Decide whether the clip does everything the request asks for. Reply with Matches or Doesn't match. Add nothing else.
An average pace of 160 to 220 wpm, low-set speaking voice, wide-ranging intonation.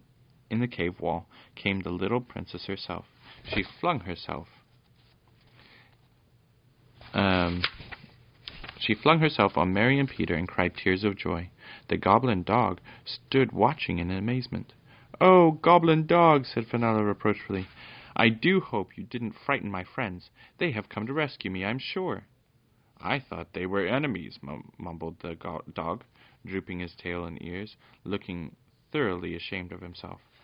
Doesn't match